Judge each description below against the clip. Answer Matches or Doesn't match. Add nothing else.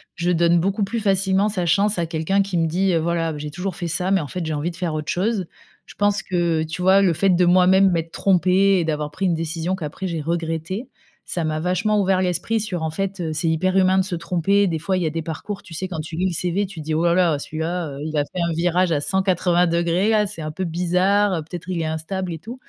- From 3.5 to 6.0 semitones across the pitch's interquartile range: Doesn't match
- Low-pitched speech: Doesn't match